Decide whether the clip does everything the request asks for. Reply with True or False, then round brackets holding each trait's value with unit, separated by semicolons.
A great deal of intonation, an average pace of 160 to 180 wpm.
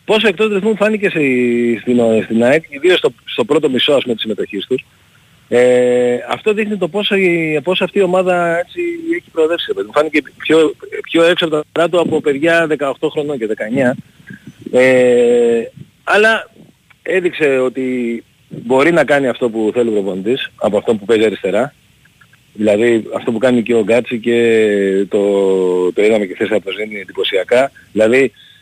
True (7.9 semitones; 170 wpm)